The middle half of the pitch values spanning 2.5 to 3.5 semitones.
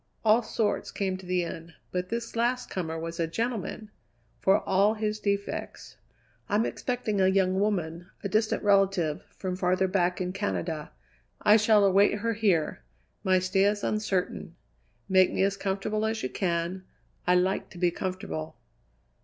Yes: average, 2.8 semitones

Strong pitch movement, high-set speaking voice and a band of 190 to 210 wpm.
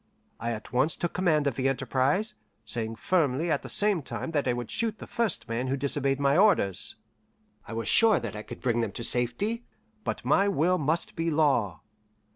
No: wide, 6.5 semitones; medium, 140 Hz; average, 200 wpm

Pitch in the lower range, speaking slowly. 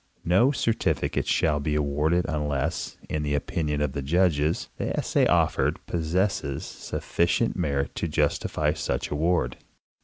Yes: very low, 75 Hz; slow, 130 wpm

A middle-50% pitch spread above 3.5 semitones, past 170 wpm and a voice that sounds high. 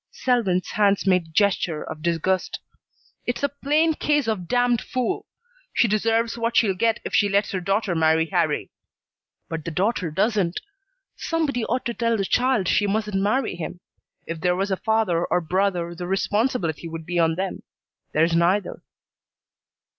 No: average, 5.0 semitones; average, 160 wpm; high, 195 Hz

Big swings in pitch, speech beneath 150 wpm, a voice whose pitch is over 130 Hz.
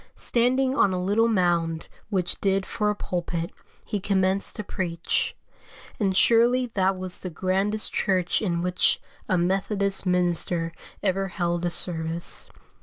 No: average, 2.7 semitones; average, 140 wpm; medium, 185 Hz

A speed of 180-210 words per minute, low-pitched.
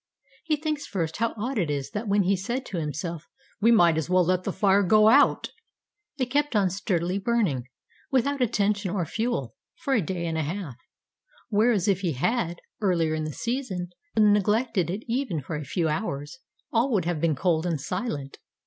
No: average, 190 wpm; high, 195 Hz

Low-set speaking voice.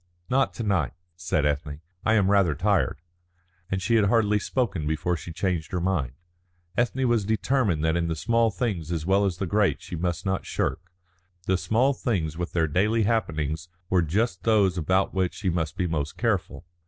Yes: very low, 95 Hz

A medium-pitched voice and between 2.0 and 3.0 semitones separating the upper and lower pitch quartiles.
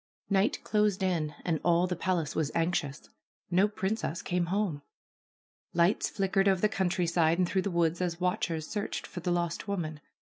Yes: medium, 180 Hz; narrow, 2.4 semitones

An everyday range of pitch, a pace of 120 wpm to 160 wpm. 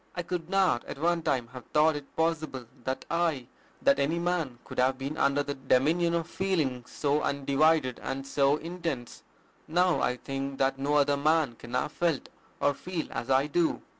No: average, 3.8 semitones; average, 185 wpm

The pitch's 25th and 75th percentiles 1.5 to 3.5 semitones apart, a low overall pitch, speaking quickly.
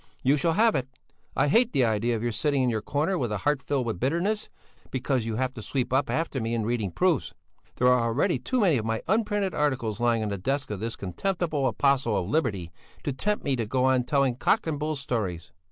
No: average, 4.7 semitones; low, 130 Hz; fast, 235 wpm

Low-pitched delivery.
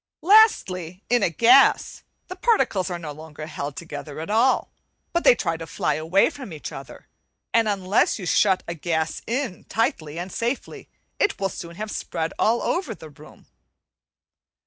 No: medium, 185 Hz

